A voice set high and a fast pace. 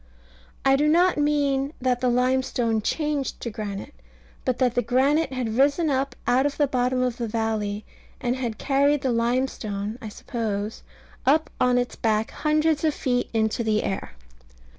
No: very high, 250 Hz; average, 165 wpm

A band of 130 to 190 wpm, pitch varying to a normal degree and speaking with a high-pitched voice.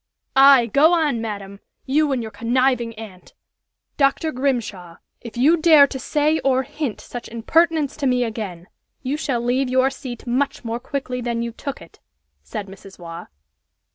Yes: average, 170 wpm; average, 3.6 semitones; very high, 250 Hz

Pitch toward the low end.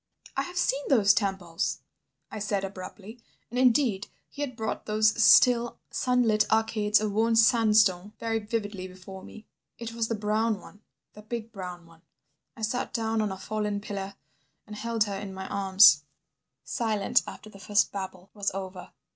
No: high, 210 Hz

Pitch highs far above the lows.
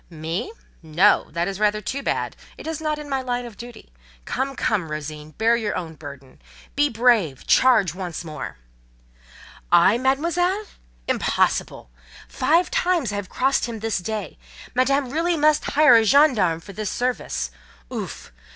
Yes: wide, 8.3 semitones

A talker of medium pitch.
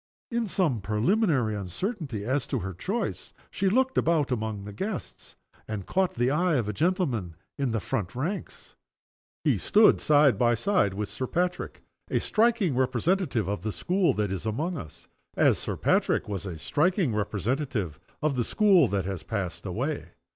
No: low, 130 Hz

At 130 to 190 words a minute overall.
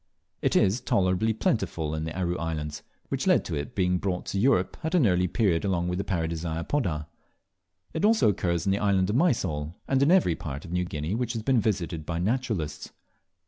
No: average, 200 wpm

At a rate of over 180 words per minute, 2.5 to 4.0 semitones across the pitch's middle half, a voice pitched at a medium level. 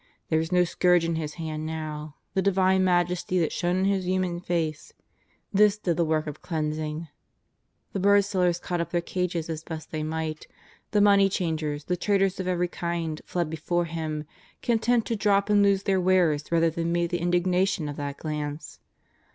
Yes: average, 190 wpm; average, 2.9 semitones; medium, 175 Hz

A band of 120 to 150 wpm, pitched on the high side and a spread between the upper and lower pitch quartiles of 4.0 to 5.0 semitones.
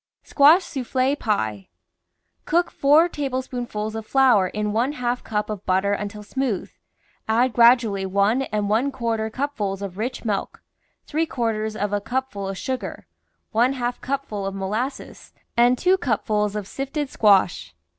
Yes: average, 145 wpm; high, 225 Hz; average, 4.3 semitones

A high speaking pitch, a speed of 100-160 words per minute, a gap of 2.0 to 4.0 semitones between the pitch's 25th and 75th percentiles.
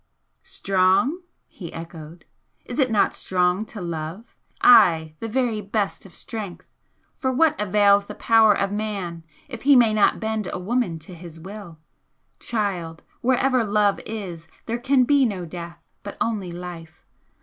No: high, 205 Hz; average, 150 wpm; average, 4.5 semitones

